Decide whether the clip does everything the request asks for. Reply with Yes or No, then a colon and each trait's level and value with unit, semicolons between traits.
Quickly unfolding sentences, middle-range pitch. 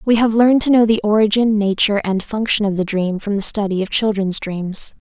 No: fast, 225 wpm; high, 210 Hz